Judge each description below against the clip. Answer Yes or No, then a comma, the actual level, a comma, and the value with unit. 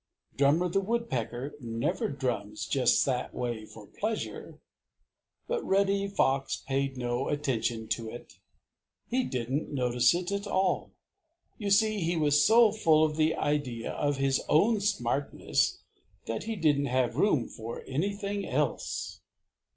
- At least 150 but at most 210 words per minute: No, slow, 135 wpm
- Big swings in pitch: Yes, wide, 8.1 semitones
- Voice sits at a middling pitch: Yes, medium, 145 Hz